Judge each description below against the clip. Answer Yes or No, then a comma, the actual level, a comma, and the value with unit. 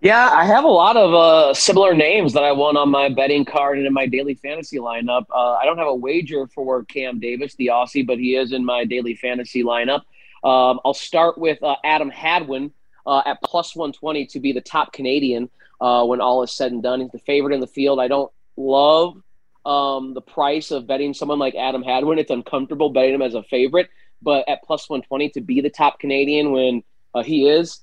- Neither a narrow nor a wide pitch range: No, narrow, 2.3 semitones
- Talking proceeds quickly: Yes, fast, 220 wpm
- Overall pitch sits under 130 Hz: No, low, 135 Hz